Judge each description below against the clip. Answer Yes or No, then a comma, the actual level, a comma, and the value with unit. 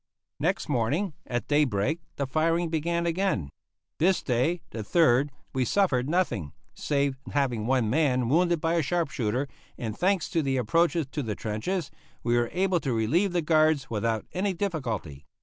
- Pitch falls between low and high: Yes, medium, 145 Hz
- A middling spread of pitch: No, wide, 6.1 semitones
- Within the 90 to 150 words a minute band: No, average, 165 wpm